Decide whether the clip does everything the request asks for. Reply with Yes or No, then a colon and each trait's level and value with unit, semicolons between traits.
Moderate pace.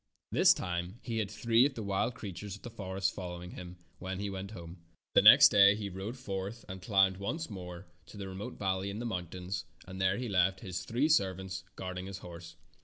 No: fast, 215 wpm